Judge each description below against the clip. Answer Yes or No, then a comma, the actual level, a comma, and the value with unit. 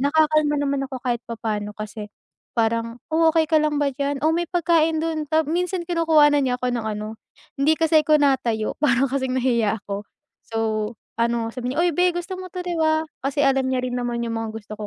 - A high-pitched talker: Yes, very high, 275 Hz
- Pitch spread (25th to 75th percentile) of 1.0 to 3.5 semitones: No, average, 5.2 semitones